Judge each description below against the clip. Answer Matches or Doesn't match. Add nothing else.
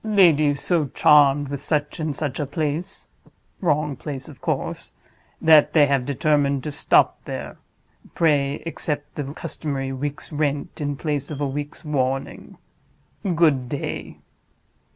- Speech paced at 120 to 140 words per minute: Matches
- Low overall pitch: Doesn't match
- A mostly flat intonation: Matches